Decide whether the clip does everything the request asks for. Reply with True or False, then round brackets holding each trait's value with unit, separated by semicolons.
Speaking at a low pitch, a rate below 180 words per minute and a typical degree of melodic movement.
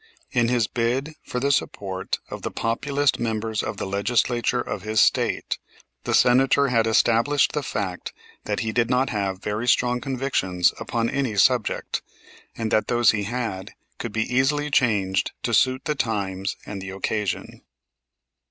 True (115 Hz; 160 wpm; 3.6 semitones)